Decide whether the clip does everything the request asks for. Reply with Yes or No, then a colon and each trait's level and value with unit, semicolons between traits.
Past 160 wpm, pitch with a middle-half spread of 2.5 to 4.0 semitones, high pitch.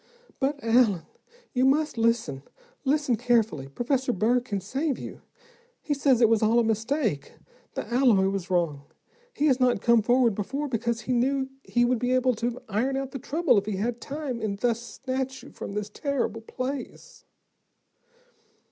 Yes: average, 170 wpm; average, 3.3 semitones; high, 240 Hz